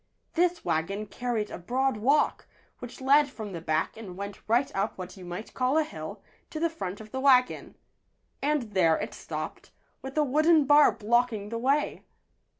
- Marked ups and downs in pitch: Yes, wide, 5.9 semitones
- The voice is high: Yes, high, 245 Hz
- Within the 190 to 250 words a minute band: No, average, 180 wpm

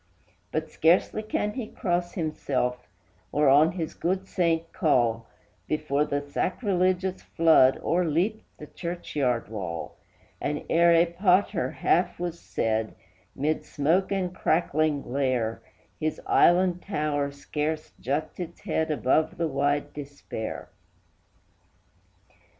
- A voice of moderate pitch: Yes, medium, 155 Hz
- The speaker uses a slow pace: Yes, slow, 115 wpm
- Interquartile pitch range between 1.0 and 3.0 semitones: No, average, 3.8 semitones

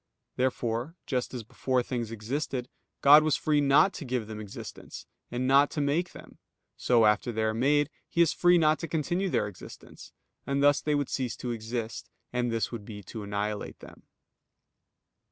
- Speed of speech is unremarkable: Yes, average, 180 wpm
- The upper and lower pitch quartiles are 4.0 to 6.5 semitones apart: Yes, average, 4.6 semitones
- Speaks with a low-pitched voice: Yes, low, 125 Hz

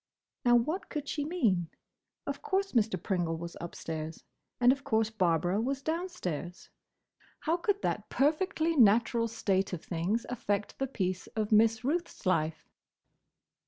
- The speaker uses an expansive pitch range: Yes, wide, 8.0 semitones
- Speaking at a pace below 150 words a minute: Yes, average, 140 wpm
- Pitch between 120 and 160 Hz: No, high, 225 Hz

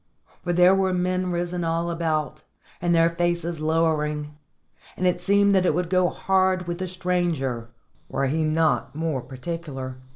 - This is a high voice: No, medium, 170 Hz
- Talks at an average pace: Yes, average, 160 wpm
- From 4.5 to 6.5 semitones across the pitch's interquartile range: No, average, 2.7 semitones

